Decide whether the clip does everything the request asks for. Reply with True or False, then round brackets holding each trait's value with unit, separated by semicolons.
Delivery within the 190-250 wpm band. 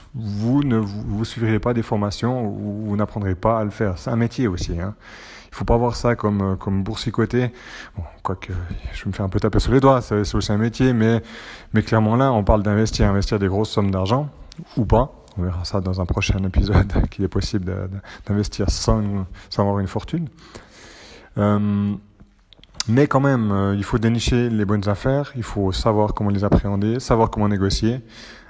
True (200 wpm)